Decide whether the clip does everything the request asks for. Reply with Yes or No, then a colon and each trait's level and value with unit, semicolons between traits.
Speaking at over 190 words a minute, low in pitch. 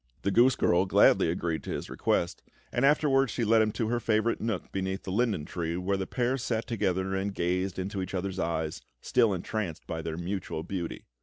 Yes: fast, 205 wpm; very low, 95 Hz